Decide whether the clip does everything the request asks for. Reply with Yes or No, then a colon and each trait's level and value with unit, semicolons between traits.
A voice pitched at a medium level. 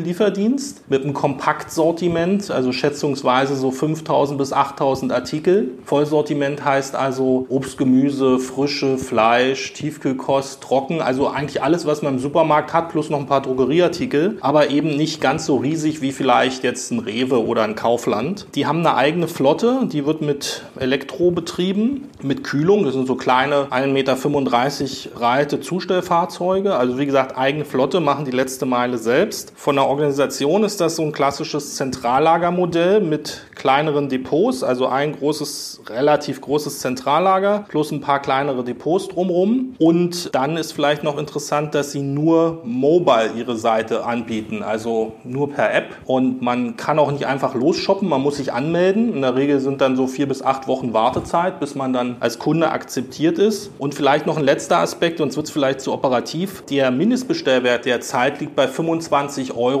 Yes: medium, 145 Hz